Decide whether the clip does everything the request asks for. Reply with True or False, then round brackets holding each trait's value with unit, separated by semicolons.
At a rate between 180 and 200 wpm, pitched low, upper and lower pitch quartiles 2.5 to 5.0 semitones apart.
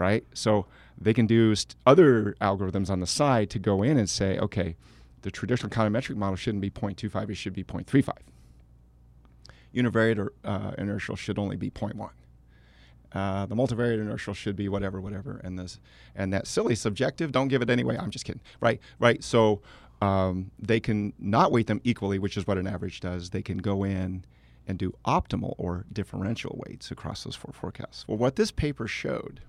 True (185 wpm; 100 Hz; 3.2 semitones)